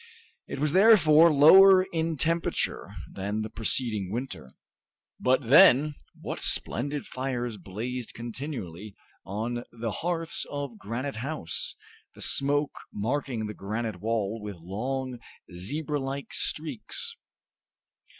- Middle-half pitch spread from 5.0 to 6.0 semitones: Yes, wide, 5.6 semitones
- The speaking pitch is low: Yes, low, 125 Hz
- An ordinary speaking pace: No, slow, 110 wpm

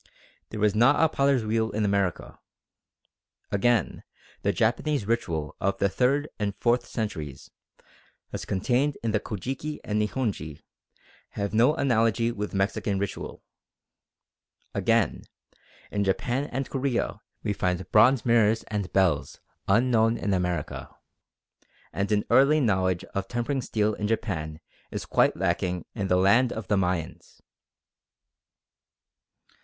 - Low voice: Yes, low, 105 Hz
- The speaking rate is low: Yes, slow, 130 wpm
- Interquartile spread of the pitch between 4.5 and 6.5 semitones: No, average, 3.8 semitones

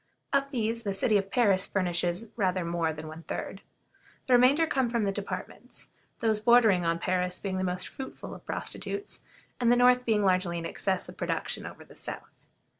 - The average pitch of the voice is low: No, high, 200 Hz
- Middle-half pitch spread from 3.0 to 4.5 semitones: No, average, 4.9 semitones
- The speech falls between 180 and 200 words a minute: Yes, average, 190 wpm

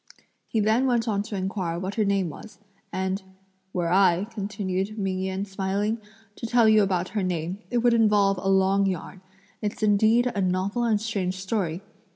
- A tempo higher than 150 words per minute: Yes, average, 180 wpm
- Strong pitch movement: No, narrow, 2.5 semitones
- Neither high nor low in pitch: No, high, 195 Hz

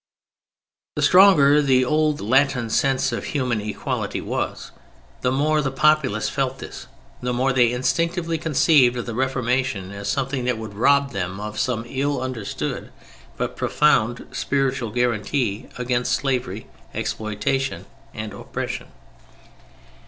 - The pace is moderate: No, slow, 130 wpm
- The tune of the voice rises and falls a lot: No, average, 3.3 semitones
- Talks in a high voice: No, low, 130 Hz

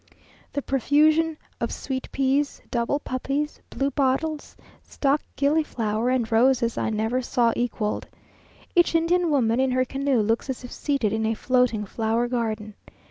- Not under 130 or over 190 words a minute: Yes, average, 140 wpm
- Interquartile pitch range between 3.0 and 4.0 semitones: Yes, average, 3.7 semitones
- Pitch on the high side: Yes, very high, 255 Hz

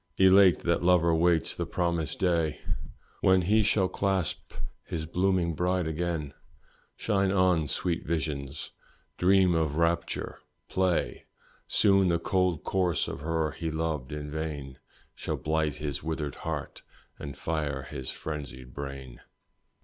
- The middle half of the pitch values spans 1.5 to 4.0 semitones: Yes, average, 3.3 semitones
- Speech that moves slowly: Yes, slow, 130 wpm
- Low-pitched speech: Yes, very low, 80 Hz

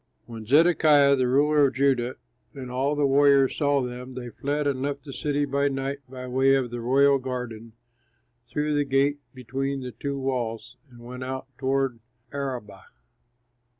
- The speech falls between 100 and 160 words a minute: No, average, 175 wpm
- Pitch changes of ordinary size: No, narrow, 1.9 semitones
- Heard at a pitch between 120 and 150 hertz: Yes, low, 135 Hz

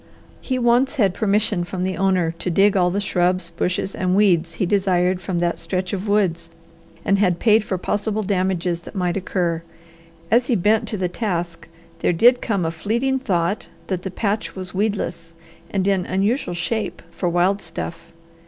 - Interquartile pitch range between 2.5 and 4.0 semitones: Yes, average, 2.9 semitones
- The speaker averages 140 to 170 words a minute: No, average, 180 wpm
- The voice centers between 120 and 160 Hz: No, high, 190 Hz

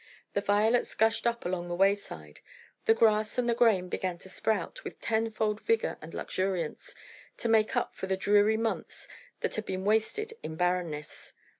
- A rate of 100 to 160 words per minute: No, average, 170 wpm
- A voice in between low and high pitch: No, high, 210 Hz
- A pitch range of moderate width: Yes, average, 3.2 semitones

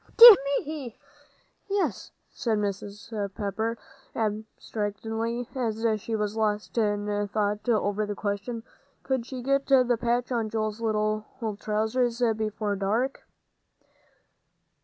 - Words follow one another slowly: Yes, slow, 110 wpm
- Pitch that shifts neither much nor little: No, narrow, 2.3 semitones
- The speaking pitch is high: Yes, high, 220 Hz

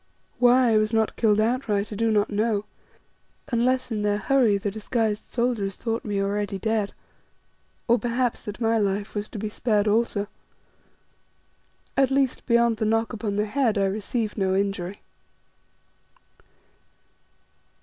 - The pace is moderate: Yes, average, 145 wpm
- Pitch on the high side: Yes, high, 215 Hz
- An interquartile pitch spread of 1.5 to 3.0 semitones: Yes, narrow, 2.4 semitones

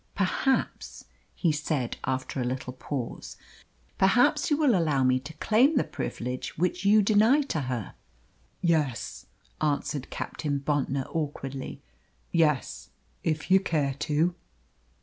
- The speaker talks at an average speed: No, slow, 125 wpm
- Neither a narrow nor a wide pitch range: No, wide, 6.3 semitones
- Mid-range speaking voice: Yes, medium, 155 Hz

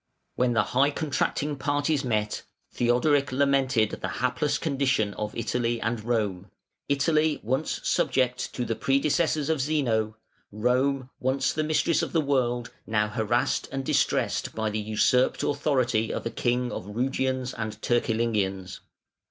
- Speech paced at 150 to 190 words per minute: No, average, 140 wpm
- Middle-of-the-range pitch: No, low, 125 Hz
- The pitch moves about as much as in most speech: Yes, average, 4.0 semitones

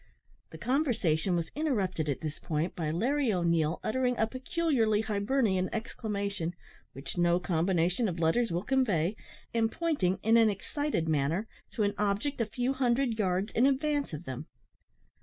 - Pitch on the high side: Yes, high, 205 Hz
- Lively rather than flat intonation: Yes, wide, 6.4 semitones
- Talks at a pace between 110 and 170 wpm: Yes, average, 155 wpm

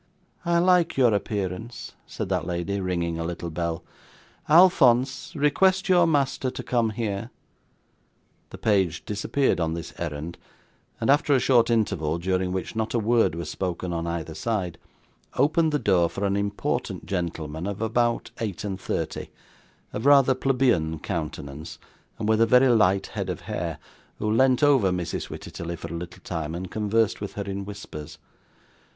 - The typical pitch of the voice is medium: No, low, 100 Hz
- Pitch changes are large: Yes, wide, 6.2 semitones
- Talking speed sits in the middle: Yes, average, 160 wpm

